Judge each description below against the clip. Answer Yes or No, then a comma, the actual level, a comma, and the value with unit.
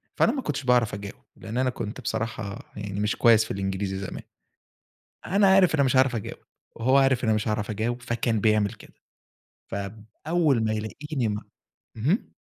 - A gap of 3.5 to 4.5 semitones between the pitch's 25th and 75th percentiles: Yes, average, 4.0 semitones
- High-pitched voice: No, low, 115 Hz